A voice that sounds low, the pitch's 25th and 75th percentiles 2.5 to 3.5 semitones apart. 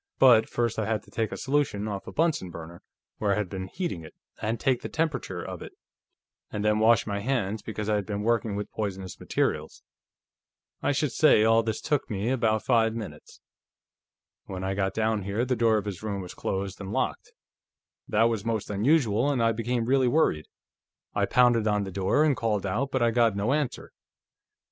Yes: low, 110 Hz; average, 3.0 semitones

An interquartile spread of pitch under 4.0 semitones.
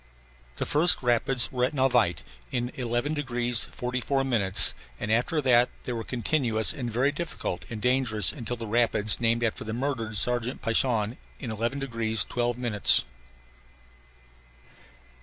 Yes: narrow, 2.5 semitones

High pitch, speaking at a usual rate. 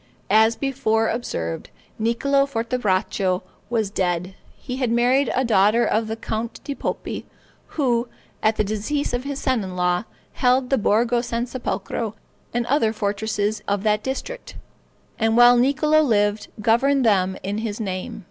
Yes: high, 225 Hz; average, 150 wpm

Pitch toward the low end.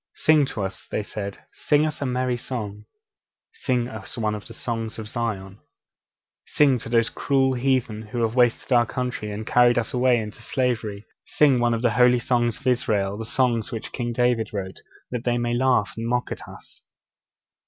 Yes: low, 120 Hz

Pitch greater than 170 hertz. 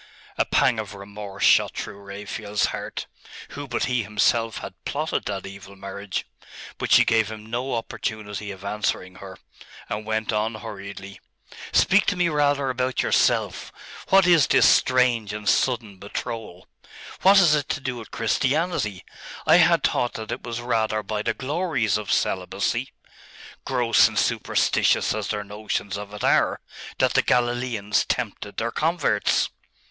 No: low, 110 Hz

